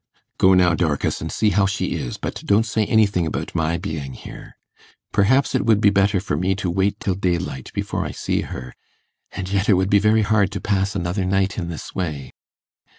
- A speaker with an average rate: No, fast, 210 wpm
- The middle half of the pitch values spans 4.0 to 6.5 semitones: No, average, 2.9 semitones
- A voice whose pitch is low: Yes, very low, 95 Hz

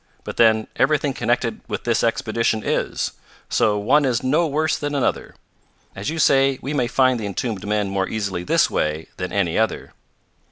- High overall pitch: No, low, 110 Hz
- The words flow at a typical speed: Yes, average, 175 wpm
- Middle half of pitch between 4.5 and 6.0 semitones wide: Yes, average, 5.1 semitones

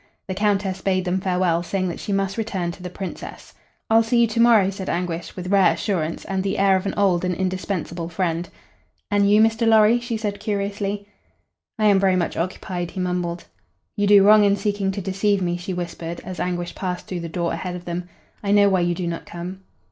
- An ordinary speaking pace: No, fast, 215 wpm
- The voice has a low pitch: No, high, 190 Hz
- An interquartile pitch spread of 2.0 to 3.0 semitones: Yes, narrow, 2.4 semitones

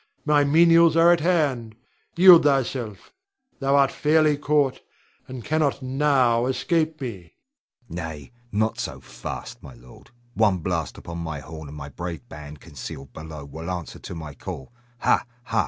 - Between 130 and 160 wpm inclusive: Yes, average, 155 wpm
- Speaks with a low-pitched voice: Yes, low, 115 Hz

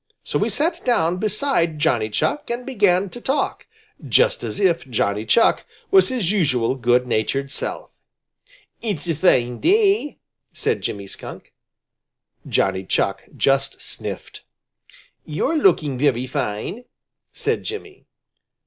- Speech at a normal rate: No, slow, 125 wpm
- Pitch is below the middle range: No, medium, 165 Hz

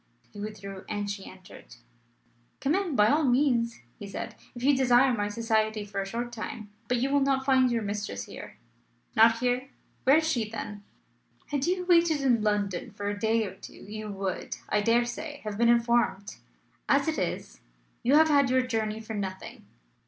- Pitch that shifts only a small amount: No, average, 4.2 semitones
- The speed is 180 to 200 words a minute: Yes, average, 190 wpm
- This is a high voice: Yes, high, 230 Hz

